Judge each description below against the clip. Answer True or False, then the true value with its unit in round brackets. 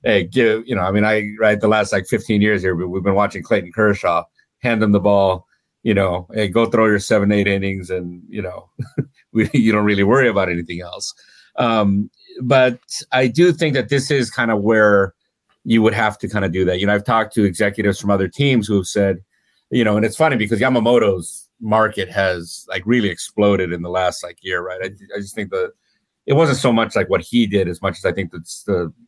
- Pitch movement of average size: True (3.0 semitones)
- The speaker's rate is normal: False (230 wpm)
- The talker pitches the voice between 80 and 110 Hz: True (105 Hz)